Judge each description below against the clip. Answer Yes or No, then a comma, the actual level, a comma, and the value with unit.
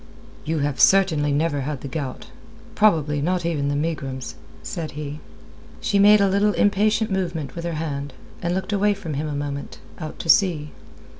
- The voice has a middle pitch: Yes, medium, 160 Hz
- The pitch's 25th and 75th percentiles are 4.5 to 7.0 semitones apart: Yes, average, 4.8 semitones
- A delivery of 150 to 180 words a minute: Yes, average, 175 wpm